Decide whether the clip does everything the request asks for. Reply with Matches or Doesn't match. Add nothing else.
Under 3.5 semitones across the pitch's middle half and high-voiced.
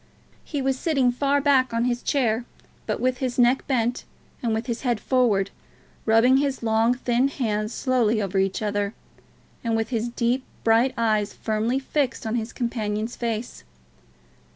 Matches